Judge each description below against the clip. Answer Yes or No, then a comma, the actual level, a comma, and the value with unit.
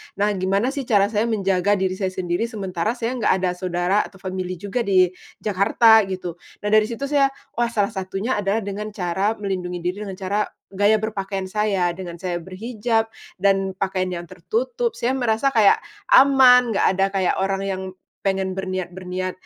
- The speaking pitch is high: Yes, high, 195 Hz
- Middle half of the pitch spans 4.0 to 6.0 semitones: No, average, 2.9 semitones